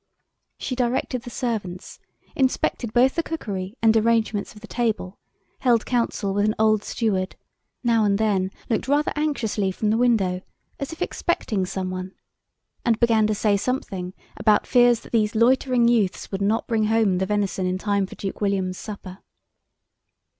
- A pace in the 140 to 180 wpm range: Yes, average, 165 wpm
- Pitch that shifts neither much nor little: Yes, average, 3.4 semitones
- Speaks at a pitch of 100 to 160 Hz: No, high, 215 Hz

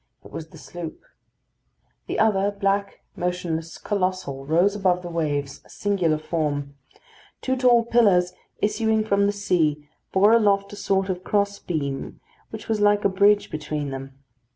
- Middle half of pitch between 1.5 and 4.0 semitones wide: No, average, 4.4 semitones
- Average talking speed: Yes, average, 155 wpm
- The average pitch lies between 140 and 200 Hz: Yes, high, 190 Hz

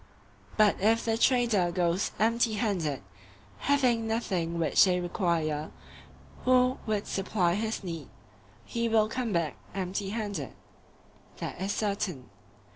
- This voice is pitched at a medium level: No, high, 205 Hz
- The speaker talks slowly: Yes, slow, 120 wpm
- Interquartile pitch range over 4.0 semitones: Yes, average, 4.5 semitones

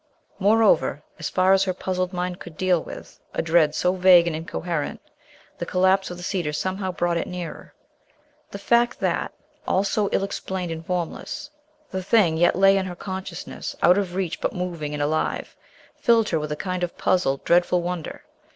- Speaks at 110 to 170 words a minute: No, average, 185 wpm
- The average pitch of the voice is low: No, medium, 180 Hz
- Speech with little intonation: Yes, narrow, 2.1 semitones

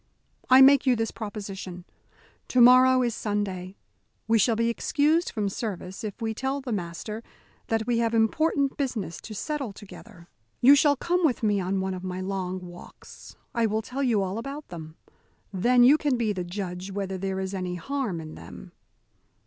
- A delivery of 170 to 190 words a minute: Yes, average, 180 wpm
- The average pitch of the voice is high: Yes, high, 215 Hz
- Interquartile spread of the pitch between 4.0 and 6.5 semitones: Yes, average, 5.1 semitones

